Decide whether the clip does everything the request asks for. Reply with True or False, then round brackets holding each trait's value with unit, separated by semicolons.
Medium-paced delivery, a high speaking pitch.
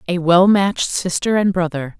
False (180 wpm; 180 Hz)